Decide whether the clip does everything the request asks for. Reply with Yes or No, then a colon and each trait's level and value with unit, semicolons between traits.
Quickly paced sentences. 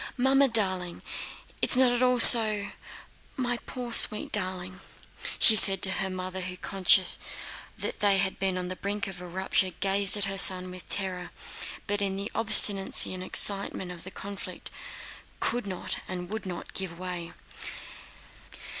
No: average, 160 wpm